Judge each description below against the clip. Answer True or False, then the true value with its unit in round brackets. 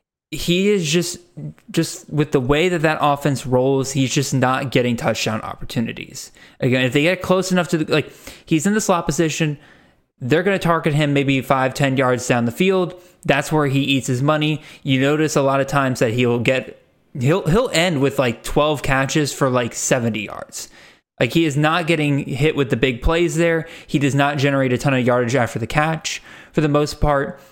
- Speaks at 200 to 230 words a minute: True (205 wpm)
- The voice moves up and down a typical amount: True (3.3 semitones)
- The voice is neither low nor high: True (145 Hz)